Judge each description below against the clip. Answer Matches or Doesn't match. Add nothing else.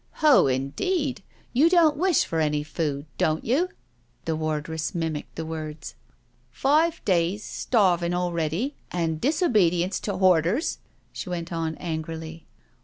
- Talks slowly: Matches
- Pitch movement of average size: Doesn't match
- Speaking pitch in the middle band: Matches